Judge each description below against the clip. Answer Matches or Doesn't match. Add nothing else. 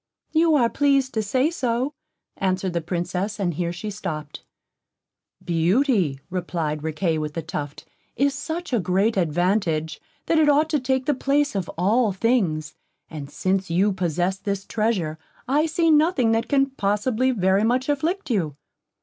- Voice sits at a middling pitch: Doesn't match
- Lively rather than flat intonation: Matches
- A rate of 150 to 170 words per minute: Matches